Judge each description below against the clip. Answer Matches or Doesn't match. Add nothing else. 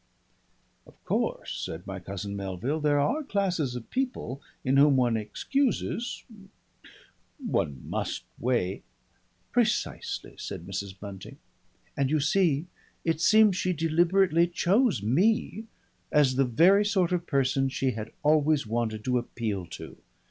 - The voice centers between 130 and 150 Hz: Matches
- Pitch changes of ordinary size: Doesn't match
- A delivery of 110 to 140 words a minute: Matches